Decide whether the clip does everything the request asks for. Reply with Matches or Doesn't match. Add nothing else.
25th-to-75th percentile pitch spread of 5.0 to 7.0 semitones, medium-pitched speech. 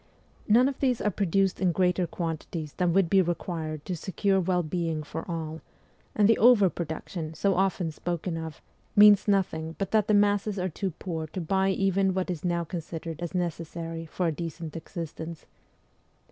Doesn't match